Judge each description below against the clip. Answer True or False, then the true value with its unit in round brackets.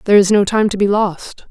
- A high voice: True (200 Hz)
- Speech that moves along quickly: True (280 wpm)